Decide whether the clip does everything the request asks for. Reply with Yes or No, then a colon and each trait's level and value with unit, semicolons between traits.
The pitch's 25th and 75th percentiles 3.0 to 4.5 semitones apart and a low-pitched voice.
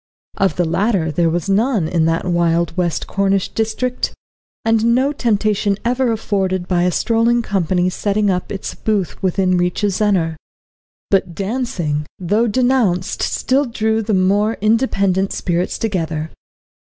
No: average, 4.0 semitones; high, 195 Hz